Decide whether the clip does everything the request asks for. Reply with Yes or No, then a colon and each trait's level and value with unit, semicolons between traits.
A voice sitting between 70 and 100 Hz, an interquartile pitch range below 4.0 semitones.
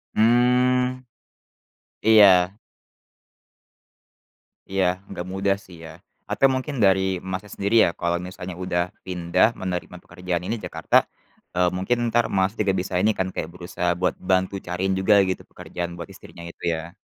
Yes: very low, 95 Hz; average, 2.9 semitones